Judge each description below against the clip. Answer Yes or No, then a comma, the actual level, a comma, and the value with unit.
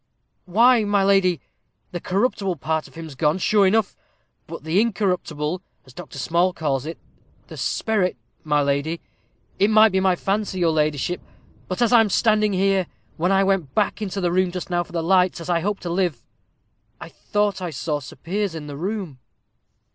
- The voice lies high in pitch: No, medium, 180 Hz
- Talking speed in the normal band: Yes, average, 185 wpm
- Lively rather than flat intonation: No, average, 3.7 semitones